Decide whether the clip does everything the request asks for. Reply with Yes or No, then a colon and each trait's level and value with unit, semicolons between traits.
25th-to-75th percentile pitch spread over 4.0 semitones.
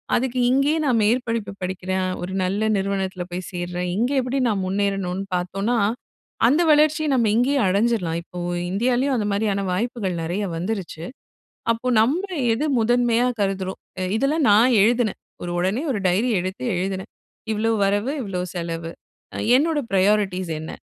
Yes: average, 4.6 semitones